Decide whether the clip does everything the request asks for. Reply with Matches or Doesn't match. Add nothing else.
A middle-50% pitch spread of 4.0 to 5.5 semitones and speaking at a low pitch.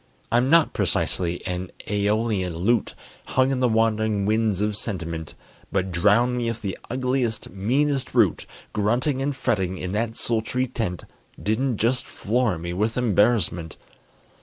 Matches